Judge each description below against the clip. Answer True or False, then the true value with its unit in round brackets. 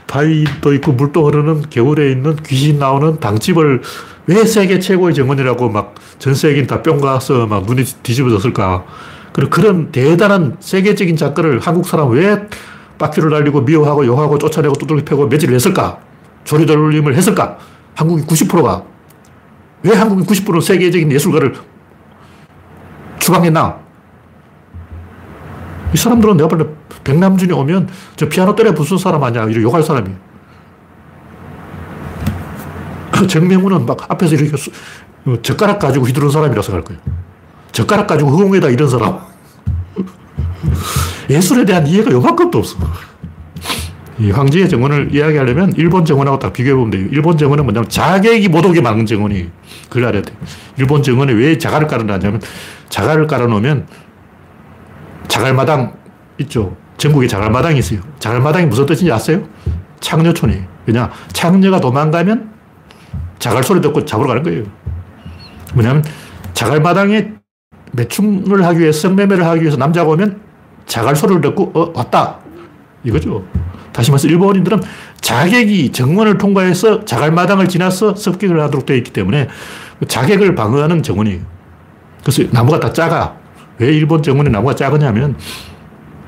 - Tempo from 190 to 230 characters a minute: False (330 characters per minute)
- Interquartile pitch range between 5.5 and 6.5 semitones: False (7.5 semitones)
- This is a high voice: False (145 Hz)